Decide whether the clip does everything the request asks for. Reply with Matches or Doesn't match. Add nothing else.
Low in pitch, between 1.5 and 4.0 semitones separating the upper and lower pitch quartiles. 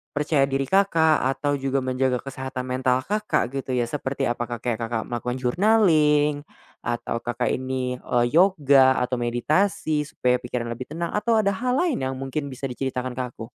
Matches